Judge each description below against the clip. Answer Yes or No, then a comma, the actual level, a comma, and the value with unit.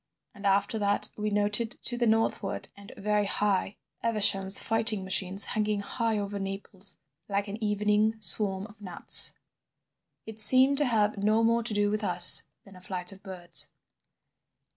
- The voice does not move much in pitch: Yes, narrow, 1.8 semitones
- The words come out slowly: No, average, 160 wpm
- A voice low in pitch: No, high, 210 Hz